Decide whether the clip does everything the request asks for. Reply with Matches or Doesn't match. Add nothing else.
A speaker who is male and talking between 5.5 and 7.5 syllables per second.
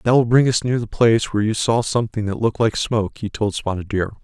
Matches